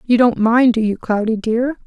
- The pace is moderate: No, fast, 225 wpm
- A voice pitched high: Yes, high, 230 Hz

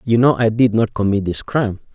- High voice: No, low, 110 Hz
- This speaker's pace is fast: Yes, fast, 245 wpm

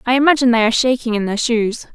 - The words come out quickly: Yes, fast, 245 wpm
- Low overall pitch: No, high, 240 Hz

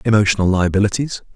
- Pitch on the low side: Yes, low, 105 Hz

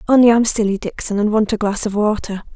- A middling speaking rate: No, fast, 235 wpm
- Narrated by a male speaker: No, female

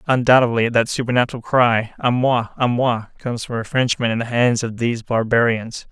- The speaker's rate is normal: Yes, average, 180 wpm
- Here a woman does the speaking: No, male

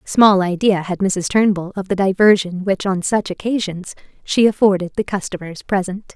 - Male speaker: No, female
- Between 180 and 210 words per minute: No, average, 165 wpm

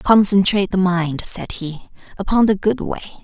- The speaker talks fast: No, average, 165 wpm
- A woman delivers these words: Yes, female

